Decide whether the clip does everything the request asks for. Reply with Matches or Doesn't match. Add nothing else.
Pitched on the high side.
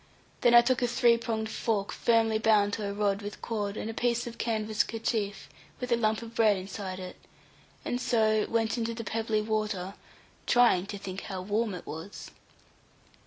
Matches